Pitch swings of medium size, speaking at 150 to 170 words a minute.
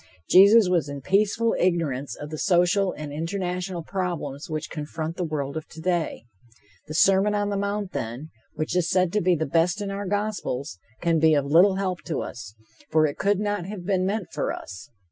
No: average, 4.2 semitones; average, 195 wpm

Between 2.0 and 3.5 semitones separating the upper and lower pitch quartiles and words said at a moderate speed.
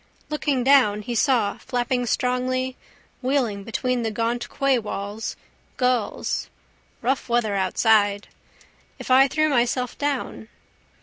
No: average, 2.9 semitones; slow, 110 wpm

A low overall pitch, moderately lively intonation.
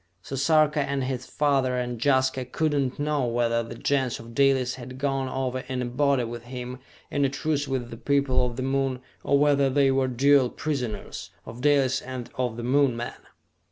No: low, 130 Hz; narrow, 2.2 semitones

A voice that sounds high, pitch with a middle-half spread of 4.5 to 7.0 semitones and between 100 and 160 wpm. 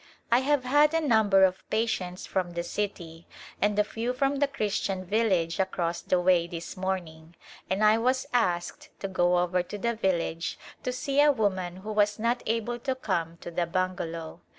No: high, 195 Hz; average, 4.8 semitones; average, 185 wpm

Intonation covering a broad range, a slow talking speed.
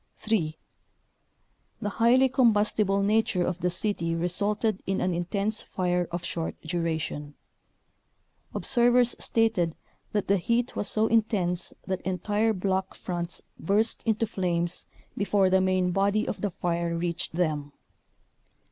No: average, 3.6 semitones; slow, 130 wpm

